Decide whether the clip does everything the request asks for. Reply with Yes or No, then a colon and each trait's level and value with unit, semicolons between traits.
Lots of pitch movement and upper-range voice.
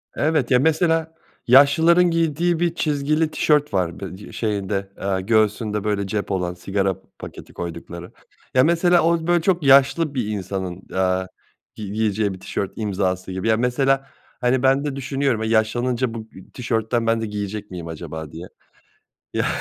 No: wide, 6.5 semitones; low, 110 Hz